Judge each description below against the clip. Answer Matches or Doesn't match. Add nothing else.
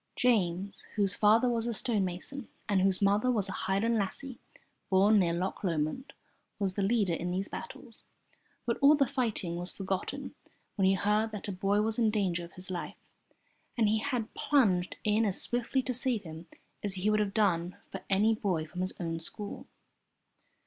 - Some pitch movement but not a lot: Matches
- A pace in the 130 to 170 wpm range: Doesn't match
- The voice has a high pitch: Matches